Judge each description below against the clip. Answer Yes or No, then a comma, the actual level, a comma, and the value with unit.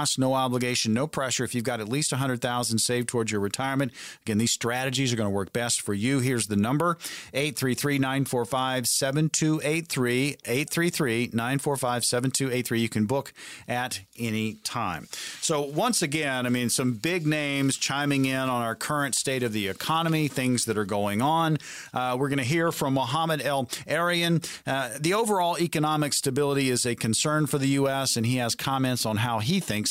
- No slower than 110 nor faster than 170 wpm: No, average, 180 wpm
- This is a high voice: No, low, 130 Hz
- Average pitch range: Yes, average, 3.5 semitones